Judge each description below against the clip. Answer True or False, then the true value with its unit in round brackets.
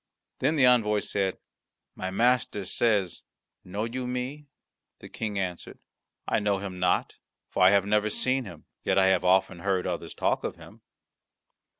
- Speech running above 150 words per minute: True (165 wpm)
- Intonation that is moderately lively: True (4.1 semitones)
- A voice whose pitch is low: True (100 Hz)